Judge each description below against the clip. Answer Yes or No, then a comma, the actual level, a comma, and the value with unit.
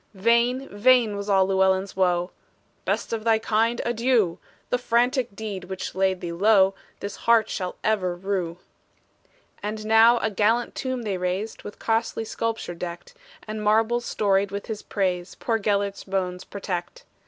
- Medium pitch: No, high, 205 Hz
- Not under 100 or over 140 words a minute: No, average, 155 wpm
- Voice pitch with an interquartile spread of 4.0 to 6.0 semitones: No, average, 3.2 semitones